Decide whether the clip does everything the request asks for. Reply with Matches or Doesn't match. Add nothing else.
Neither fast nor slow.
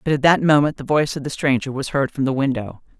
Doesn't match